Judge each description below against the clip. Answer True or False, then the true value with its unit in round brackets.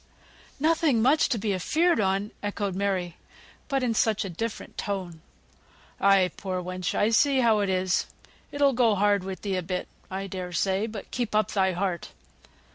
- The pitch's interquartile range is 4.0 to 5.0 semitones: False (3.5 semitones)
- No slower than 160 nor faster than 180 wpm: True (175 wpm)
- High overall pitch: True (200 Hz)